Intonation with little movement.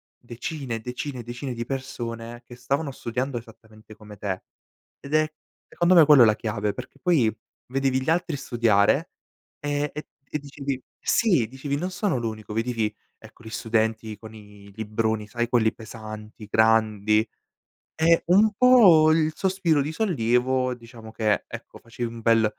No: average, 4.5 semitones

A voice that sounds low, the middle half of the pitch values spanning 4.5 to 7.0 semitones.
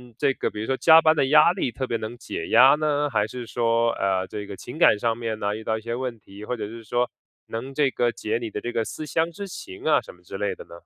Yes: low, 120 Hz; average, 5.1 semitones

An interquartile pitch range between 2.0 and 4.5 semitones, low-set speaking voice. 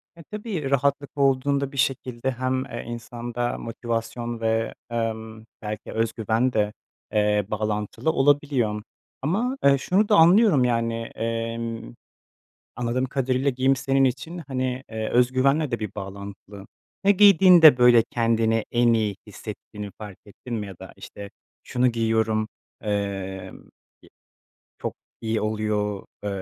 Yes: average, 3.6 semitones; low, 120 Hz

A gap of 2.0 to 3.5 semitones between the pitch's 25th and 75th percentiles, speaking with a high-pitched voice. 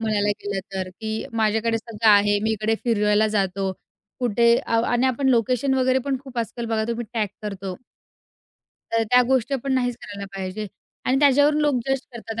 Yes: average, 3.2 semitones; high, 225 Hz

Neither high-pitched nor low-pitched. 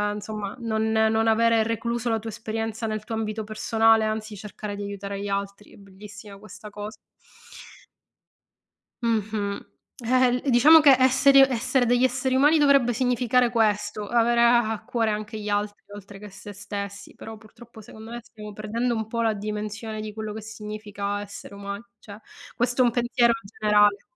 No: high, 220 Hz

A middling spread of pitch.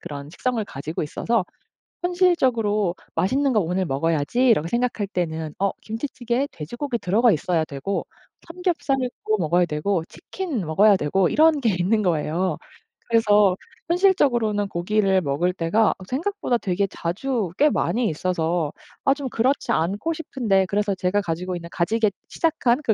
No: wide, 6.2 semitones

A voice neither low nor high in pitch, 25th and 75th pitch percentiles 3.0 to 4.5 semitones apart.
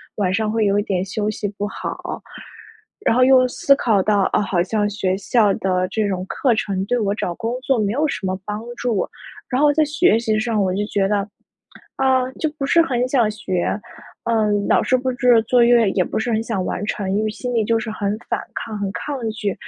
No: high, 215 Hz; average, 3.5 semitones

